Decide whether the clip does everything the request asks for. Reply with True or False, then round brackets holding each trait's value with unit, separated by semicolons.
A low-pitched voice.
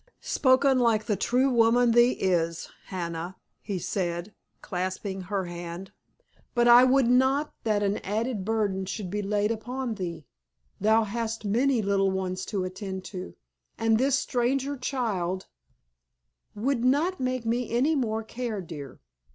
False (220 Hz)